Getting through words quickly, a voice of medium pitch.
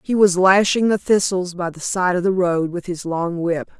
Yes: fast, 235 wpm; medium, 180 Hz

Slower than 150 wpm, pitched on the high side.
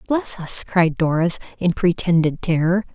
No: average, 140 wpm; medium, 175 Hz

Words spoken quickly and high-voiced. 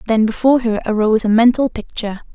No: average, 180 wpm; high, 225 Hz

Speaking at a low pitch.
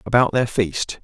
Yes: low, 115 Hz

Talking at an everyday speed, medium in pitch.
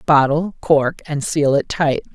Yes: average, 170 wpm; medium, 150 Hz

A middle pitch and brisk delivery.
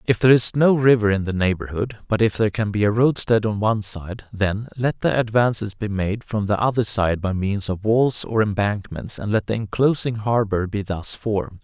No: low, 105 Hz; fast, 215 wpm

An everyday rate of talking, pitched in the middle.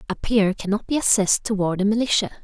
No: average, 195 wpm; high, 210 Hz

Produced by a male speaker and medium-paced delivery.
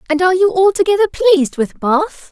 No: female; average, 180 wpm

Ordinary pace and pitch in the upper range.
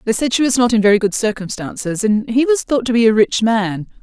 No: fast, 270 wpm; high, 225 Hz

